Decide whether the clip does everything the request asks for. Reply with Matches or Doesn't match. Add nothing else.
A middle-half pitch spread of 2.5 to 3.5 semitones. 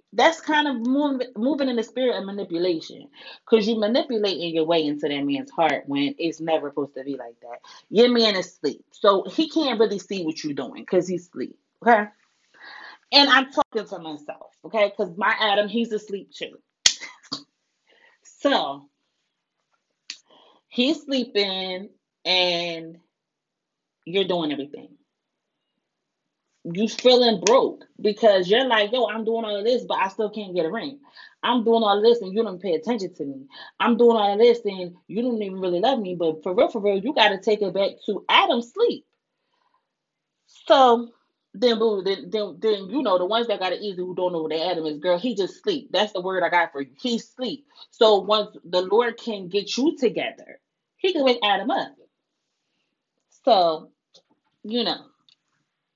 Doesn't match